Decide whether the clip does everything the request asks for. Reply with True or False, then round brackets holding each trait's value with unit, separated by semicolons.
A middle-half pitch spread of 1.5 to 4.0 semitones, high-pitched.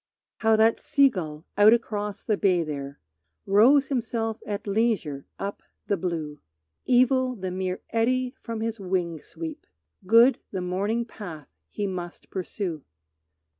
False (4.4 semitones; 205 Hz)